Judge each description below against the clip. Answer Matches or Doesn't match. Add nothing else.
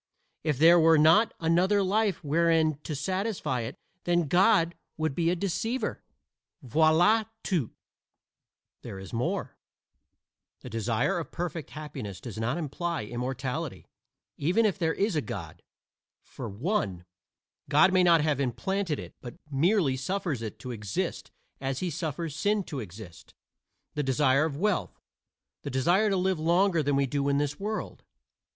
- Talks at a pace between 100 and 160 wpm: Matches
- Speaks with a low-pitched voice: Doesn't match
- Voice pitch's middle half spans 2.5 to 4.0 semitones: Doesn't match